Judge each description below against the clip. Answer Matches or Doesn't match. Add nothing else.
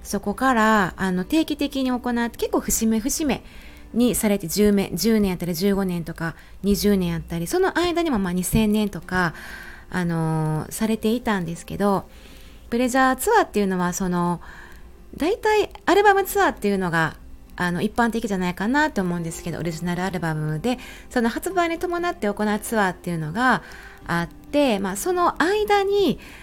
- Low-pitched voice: Doesn't match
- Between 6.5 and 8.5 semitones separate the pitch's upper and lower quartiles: Matches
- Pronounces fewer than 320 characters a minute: Matches